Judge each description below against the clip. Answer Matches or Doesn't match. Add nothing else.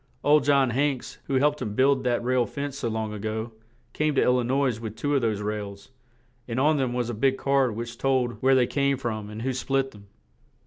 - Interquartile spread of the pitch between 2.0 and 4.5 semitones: Matches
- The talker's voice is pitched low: Matches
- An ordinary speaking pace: Doesn't match